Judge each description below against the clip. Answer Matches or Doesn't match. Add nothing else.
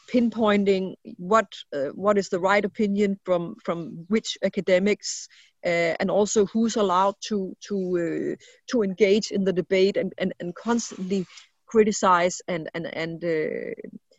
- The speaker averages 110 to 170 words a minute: Matches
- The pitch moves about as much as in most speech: Matches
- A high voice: Matches